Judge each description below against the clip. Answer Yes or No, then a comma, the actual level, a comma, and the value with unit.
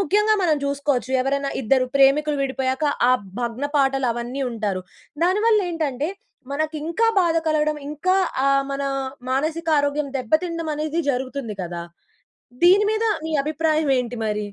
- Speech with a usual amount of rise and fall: Yes, average, 3.5 semitones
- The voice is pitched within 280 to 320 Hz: Yes, very high, 285 Hz